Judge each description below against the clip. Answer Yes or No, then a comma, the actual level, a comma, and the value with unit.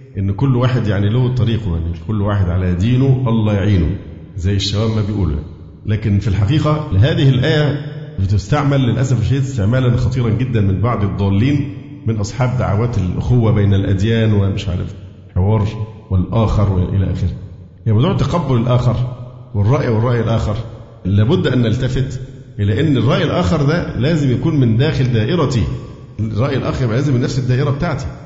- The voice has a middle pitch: No, low, 115 Hz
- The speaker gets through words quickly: Yes, fast, 150 wpm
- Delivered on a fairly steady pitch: No, average, 4.5 semitones